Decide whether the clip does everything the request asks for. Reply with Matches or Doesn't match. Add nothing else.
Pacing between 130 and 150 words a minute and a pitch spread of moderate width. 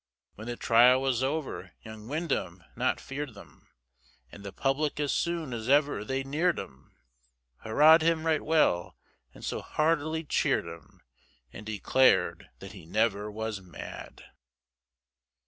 Doesn't match